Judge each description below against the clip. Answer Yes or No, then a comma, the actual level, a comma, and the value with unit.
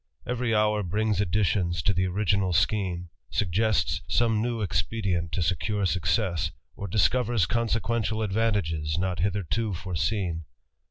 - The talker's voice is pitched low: Yes, low, 100 Hz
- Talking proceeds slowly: Yes, slow, 120 wpm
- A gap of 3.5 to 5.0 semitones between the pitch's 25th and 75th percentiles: Yes, average, 3.8 semitones